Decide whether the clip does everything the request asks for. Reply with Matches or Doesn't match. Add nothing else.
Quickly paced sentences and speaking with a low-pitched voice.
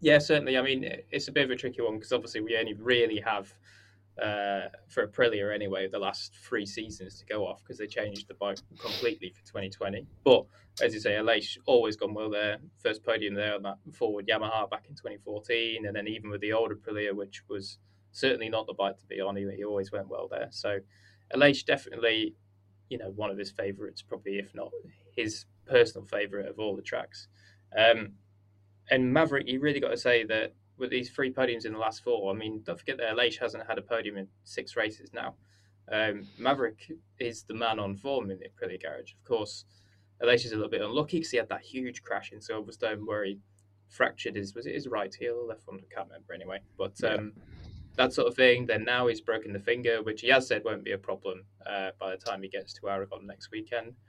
Matches